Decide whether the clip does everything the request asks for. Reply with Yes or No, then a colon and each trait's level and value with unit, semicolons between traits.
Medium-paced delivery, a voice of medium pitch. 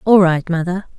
Yes: average, 185 wpm; medium, 180 Hz